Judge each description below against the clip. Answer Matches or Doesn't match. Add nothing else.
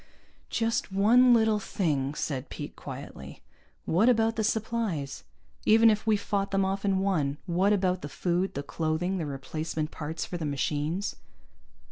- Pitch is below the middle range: Doesn't match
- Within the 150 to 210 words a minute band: Matches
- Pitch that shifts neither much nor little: Doesn't match